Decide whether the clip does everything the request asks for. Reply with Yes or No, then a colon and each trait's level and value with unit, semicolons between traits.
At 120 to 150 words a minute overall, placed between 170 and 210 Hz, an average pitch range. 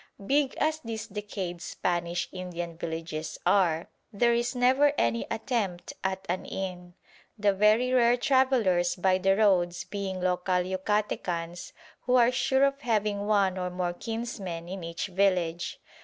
Yes: average, 140 wpm; high, 190 Hz; average, 4.7 semitones